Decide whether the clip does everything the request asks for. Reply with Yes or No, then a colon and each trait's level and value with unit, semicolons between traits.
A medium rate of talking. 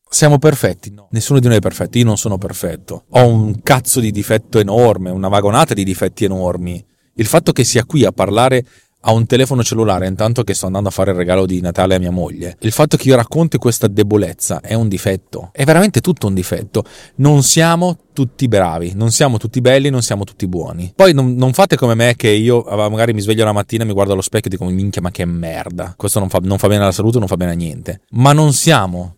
No: fast, 230 wpm